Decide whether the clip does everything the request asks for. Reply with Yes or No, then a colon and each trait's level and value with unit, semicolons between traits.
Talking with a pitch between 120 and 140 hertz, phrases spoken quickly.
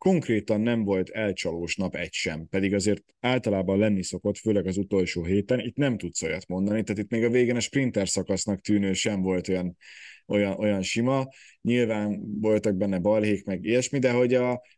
No: low, 105 Hz; fast, 185 wpm